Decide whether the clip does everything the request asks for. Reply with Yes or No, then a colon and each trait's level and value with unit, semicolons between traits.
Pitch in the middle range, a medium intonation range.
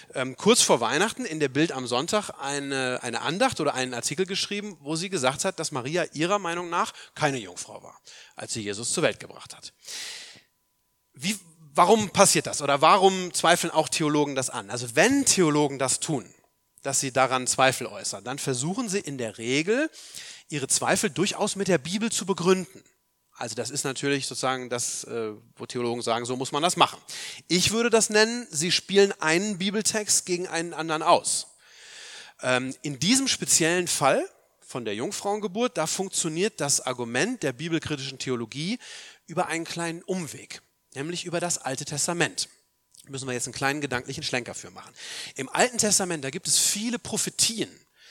No: medium, 160 Hz; wide, 6.6 semitones